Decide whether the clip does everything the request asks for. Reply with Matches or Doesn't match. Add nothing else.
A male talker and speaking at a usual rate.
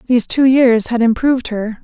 Doesn't match